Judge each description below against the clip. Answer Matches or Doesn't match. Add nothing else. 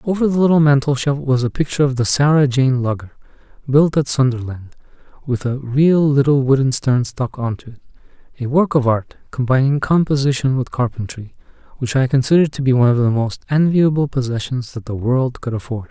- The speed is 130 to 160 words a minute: Doesn't match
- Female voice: Doesn't match